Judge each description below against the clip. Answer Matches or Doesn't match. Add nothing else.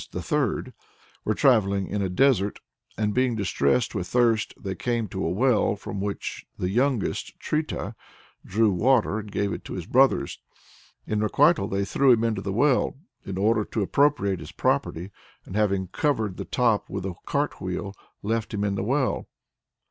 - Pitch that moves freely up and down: Doesn't match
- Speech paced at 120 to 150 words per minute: Doesn't match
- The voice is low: Matches